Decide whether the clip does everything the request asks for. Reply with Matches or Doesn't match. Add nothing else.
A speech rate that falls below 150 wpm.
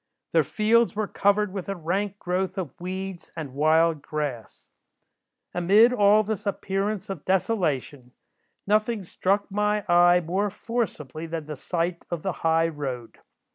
Matches